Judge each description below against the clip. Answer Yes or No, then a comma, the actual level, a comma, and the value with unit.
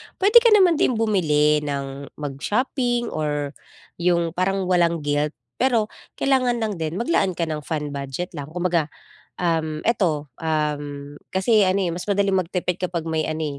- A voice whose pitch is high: No, medium, 170 Hz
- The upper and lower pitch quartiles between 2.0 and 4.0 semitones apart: No, average, 5.0 semitones